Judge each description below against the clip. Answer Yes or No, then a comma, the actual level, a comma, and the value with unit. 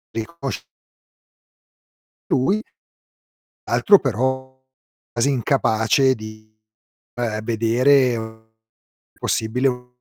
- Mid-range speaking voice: No, low, 125 Hz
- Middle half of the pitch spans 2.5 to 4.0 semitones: Yes, average, 2.9 semitones